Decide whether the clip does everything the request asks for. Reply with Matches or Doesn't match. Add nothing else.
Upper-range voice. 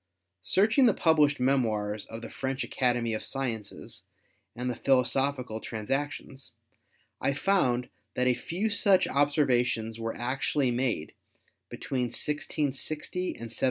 Doesn't match